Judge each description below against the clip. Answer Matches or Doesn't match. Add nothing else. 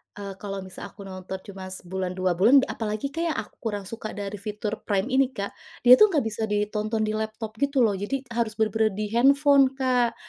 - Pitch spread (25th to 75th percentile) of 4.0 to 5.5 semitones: Doesn't match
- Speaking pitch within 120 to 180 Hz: Doesn't match